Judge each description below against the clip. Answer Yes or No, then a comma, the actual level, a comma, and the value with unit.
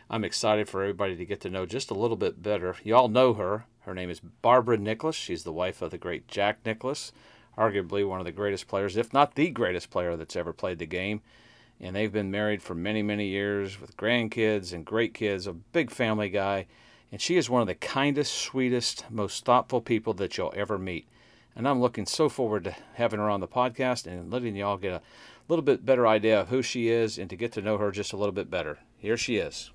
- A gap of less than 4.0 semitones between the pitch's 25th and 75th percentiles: Yes, average, 3.4 semitones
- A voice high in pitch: No, low, 105 Hz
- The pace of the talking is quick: Yes, fast, 230 wpm